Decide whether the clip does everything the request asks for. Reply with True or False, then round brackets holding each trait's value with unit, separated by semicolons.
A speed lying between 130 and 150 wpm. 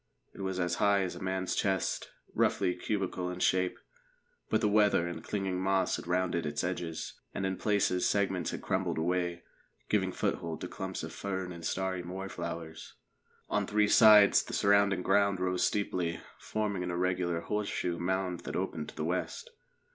False (170 wpm)